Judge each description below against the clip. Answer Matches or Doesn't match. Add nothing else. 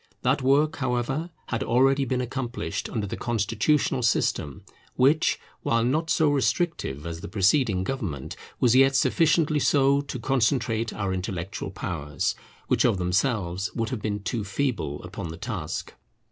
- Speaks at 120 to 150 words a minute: Matches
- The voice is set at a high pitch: Doesn't match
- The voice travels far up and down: Matches